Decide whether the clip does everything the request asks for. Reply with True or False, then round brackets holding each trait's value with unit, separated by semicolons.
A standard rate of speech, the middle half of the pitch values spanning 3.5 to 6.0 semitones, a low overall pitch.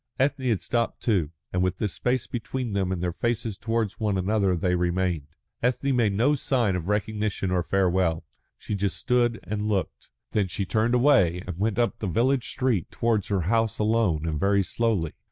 True (190 wpm; 4.1 semitones; 105 Hz)